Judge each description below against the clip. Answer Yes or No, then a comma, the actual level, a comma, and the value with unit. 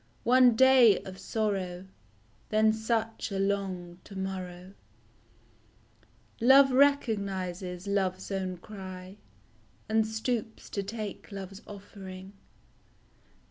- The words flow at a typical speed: No, slow, 95 wpm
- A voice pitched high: Yes, high, 200 Hz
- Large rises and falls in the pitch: No, average, 2.9 semitones